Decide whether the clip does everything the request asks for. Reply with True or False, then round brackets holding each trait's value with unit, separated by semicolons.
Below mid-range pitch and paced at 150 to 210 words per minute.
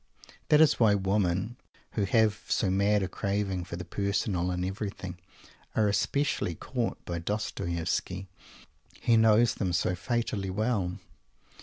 False (100 Hz; 135 wpm)